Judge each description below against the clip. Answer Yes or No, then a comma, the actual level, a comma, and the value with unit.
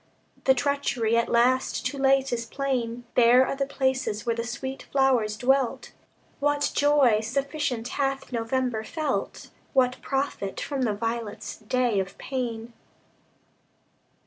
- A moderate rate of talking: No, slow, 130 wpm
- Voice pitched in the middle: No, very high, 255 Hz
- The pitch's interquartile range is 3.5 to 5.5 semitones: No, average, 2.8 semitones